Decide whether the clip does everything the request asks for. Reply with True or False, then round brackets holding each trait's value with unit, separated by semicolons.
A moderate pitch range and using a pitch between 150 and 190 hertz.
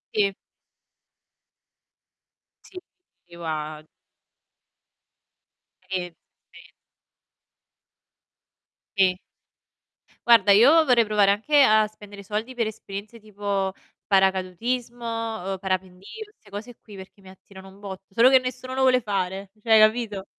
False (3.6 semitones; 205 Hz)